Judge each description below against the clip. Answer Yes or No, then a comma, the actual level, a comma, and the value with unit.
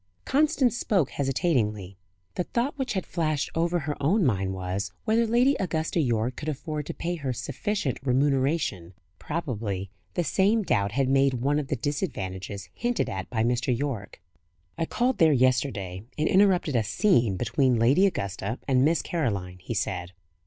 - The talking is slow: No, average, 160 wpm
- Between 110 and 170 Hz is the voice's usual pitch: Yes, low, 135 Hz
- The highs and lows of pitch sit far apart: Yes, wide, 7.6 semitones